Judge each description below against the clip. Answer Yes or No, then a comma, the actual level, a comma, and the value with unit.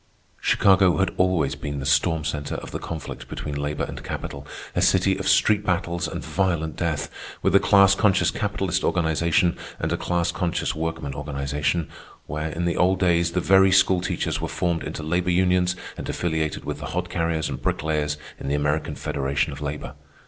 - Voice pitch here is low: Yes, very low, 85 Hz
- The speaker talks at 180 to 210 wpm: Yes, average, 185 wpm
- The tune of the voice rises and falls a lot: No, average, 3.3 semitones